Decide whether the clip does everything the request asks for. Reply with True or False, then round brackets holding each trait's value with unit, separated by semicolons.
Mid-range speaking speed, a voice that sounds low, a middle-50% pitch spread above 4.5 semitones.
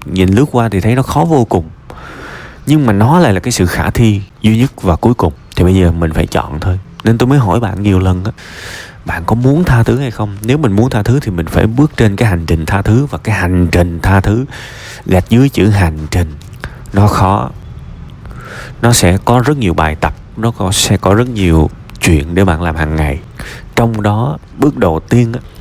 True (230 wpm; 105 Hz; 5.0 semitones)